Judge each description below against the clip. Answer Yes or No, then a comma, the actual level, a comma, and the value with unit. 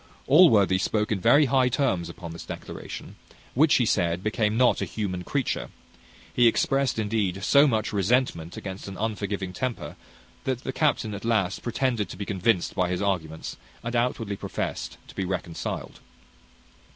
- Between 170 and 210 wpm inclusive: No, average, 160 wpm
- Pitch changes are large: No, average, 4.8 semitones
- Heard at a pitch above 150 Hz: No, low, 105 Hz